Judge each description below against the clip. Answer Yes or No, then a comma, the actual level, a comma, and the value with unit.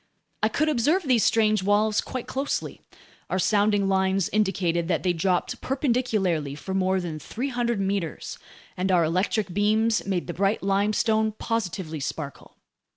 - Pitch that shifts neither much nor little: Yes, average, 3.3 semitones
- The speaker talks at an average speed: Yes, average, 145 wpm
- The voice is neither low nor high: No, high, 200 Hz